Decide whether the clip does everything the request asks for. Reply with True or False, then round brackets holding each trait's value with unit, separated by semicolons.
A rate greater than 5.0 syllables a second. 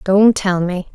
False (3.5 syllables/s)